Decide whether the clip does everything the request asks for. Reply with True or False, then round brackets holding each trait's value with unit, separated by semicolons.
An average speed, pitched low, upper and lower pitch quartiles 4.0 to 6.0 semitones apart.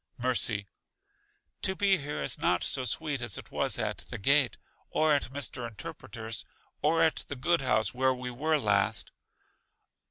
True (160 wpm; 130 Hz; 4.6 semitones)